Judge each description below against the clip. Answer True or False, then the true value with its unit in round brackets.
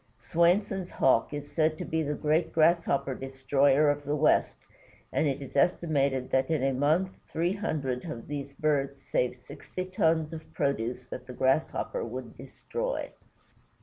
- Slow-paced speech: False (155 wpm)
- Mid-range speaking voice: True (145 Hz)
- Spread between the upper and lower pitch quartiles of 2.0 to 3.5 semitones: True (3.2 semitones)